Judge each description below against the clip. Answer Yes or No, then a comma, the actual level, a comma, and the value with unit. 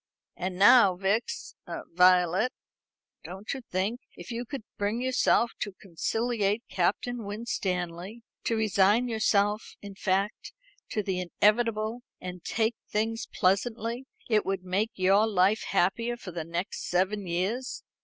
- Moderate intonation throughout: Yes, average, 3.6 semitones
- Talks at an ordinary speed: No, slow, 130 wpm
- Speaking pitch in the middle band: No, high, 205 Hz